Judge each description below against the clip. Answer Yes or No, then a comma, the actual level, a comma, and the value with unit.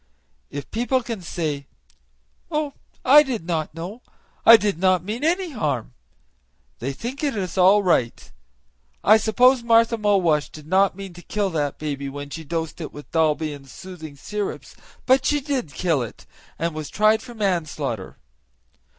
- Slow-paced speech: No, average, 160 wpm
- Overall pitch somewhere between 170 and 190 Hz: Yes, medium, 185 Hz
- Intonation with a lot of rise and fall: Yes, wide, 6.9 semitones